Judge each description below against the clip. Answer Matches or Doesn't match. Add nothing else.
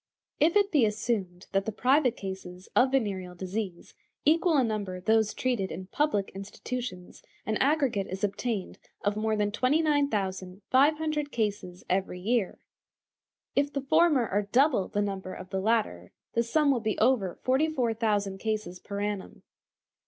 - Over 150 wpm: Doesn't match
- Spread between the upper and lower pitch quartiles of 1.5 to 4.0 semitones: Doesn't match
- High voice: Matches